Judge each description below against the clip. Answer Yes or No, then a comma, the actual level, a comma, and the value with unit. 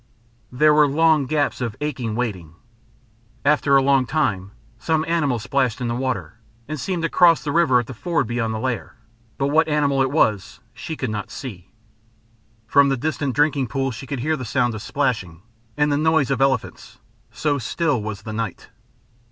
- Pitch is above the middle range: No, low, 135 Hz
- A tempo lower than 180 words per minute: No, average, 185 wpm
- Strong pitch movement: No, average, 4.2 semitones